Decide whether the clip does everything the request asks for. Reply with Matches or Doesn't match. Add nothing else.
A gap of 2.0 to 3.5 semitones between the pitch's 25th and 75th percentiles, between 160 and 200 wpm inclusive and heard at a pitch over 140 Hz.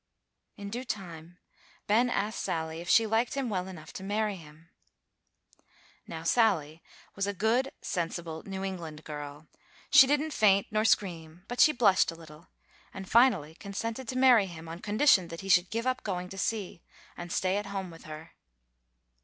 Doesn't match